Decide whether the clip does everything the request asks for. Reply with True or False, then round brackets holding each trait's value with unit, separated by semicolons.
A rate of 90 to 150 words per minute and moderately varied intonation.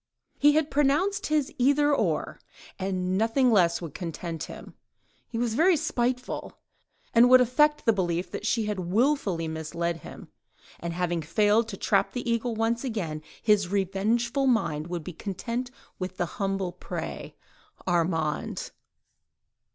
False (135 wpm; 6.1 semitones)